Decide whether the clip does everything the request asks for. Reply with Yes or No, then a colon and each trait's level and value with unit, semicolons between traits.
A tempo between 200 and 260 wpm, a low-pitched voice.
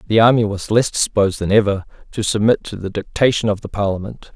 Yes: fast, 205 wpm; low, 105 Hz